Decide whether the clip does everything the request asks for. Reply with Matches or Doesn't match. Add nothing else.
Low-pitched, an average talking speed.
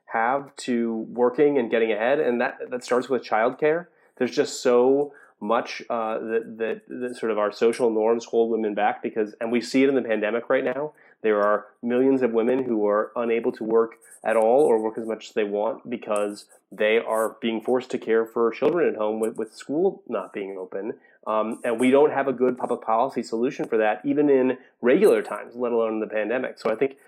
Doesn't match